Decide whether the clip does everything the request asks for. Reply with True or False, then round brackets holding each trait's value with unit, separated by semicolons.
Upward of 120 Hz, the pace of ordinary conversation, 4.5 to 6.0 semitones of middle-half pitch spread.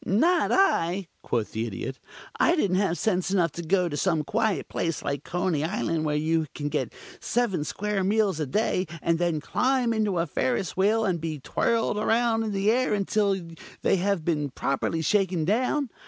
True (185 Hz; 185 wpm; 5.1 semitones)